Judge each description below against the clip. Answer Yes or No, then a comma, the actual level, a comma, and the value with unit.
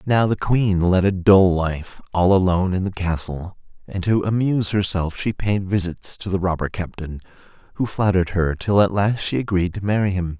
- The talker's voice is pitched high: No, very low, 95 Hz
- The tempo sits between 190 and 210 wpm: Yes, average, 195 wpm